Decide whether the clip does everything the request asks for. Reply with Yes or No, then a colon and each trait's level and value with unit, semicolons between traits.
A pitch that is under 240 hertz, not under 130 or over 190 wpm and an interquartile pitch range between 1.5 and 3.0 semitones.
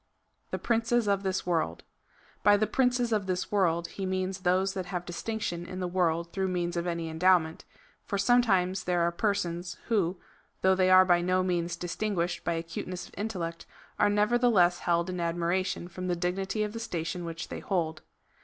Yes: medium, 185 Hz; average, 185 wpm; narrow, 2.5 semitones